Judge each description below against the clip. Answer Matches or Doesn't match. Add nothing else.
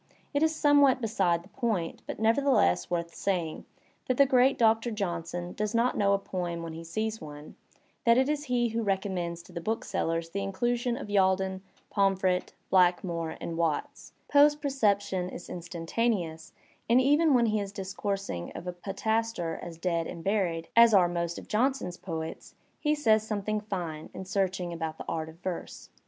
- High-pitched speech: Matches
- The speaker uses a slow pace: Doesn't match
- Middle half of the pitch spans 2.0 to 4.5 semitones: Doesn't match